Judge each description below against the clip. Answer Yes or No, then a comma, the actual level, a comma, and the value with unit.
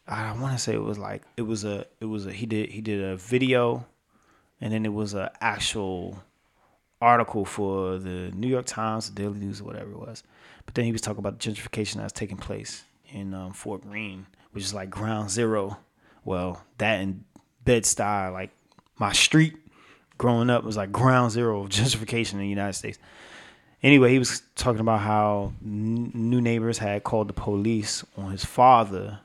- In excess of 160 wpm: Yes, average, 195 wpm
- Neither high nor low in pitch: No, low, 105 Hz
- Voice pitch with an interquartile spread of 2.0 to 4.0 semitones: Yes, average, 2.7 semitones